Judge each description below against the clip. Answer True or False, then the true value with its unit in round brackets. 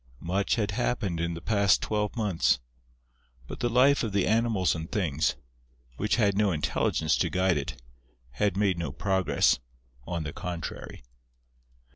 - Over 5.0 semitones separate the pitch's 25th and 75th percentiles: False (4.0 semitones)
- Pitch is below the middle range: True (95 Hz)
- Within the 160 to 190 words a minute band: False (150 wpm)